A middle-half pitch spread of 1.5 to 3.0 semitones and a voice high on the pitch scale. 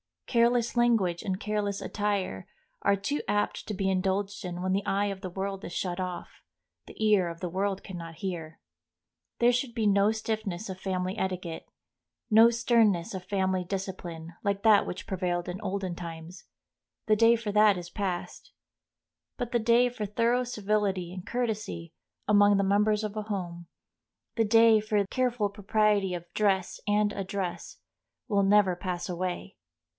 Yes: average, 2.7 semitones; high, 200 Hz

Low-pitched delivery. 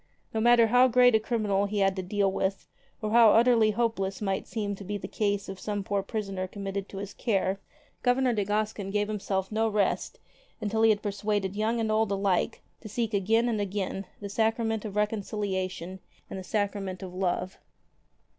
No: high, 205 Hz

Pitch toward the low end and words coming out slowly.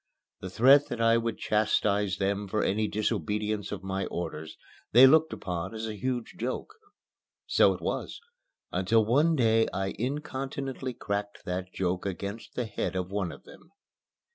No: low, 105 Hz; average, 160 wpm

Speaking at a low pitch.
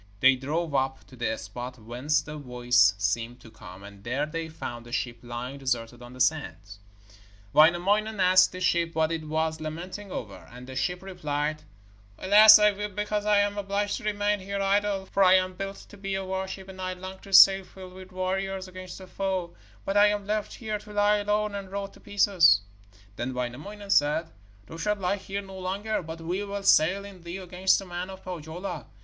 No: medium, 185 Hz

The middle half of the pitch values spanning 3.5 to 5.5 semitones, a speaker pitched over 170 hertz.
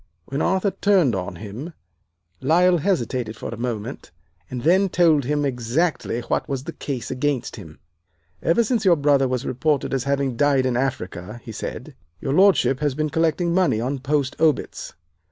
No: average, 4.8 semitones; medium, 140 Hz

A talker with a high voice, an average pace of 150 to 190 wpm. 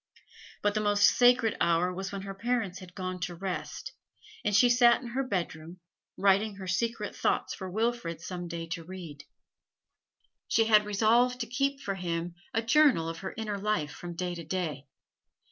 Yes: high, 195 Hz; average, 180 wpm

